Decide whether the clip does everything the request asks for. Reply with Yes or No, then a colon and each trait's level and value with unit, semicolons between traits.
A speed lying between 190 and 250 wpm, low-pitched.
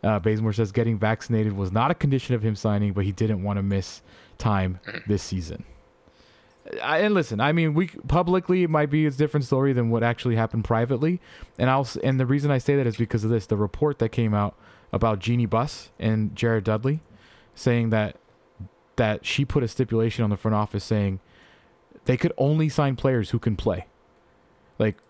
Yes: average, 200 wpm; low, 115 Hz